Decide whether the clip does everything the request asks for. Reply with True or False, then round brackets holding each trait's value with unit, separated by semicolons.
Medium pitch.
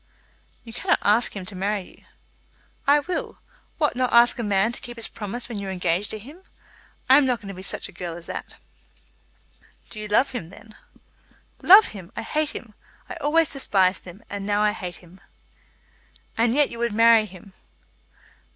False (215 Hz)